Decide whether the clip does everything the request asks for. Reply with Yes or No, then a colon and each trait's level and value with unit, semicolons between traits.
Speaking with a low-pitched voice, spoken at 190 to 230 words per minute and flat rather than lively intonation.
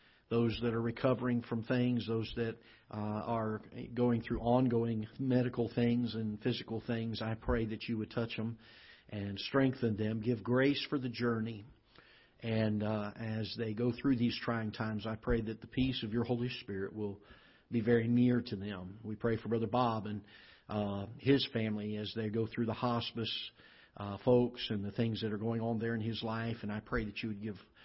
Yes: low, 115 Hz; average, 200 wpm; narrow, 1.7 semitones